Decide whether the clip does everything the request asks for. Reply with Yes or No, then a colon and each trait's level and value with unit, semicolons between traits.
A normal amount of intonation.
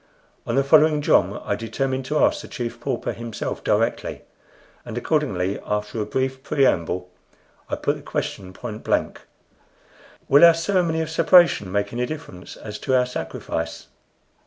No: wide, 6.2 semitones